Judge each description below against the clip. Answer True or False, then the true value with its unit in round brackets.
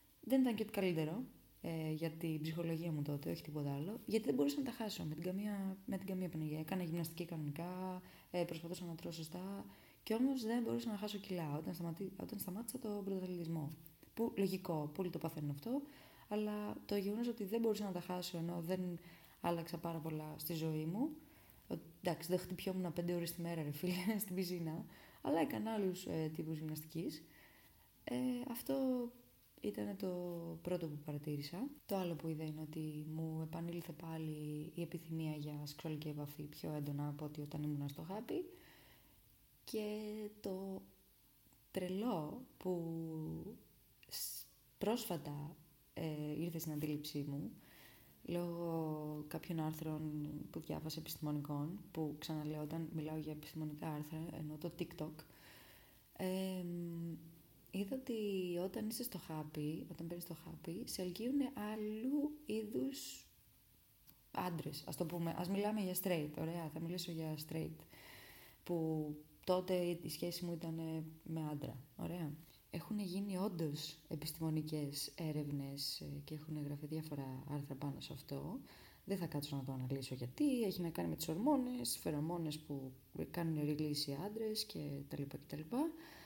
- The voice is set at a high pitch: False (165 Hz)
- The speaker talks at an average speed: True (150 wpm)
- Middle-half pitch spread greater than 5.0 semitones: False (3.8 semitones)